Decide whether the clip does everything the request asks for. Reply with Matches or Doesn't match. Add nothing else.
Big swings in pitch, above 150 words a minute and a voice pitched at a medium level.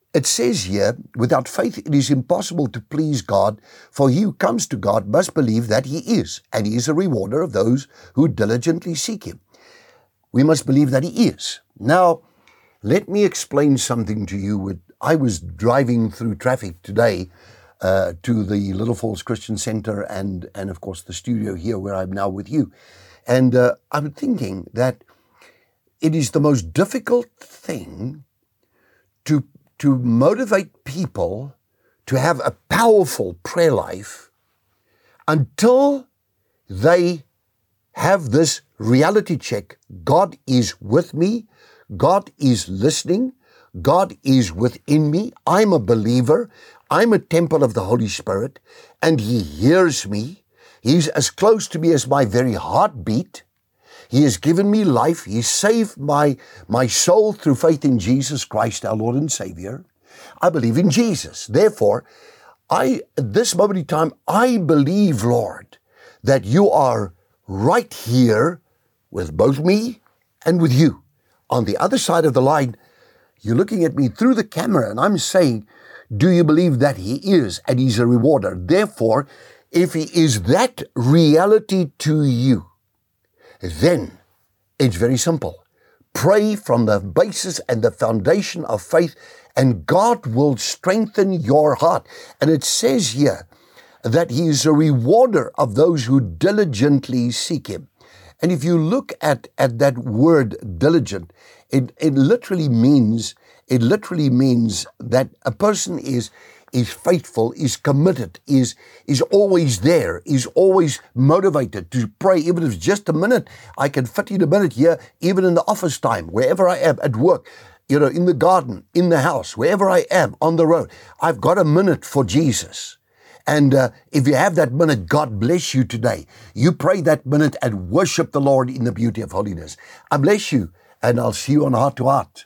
Matches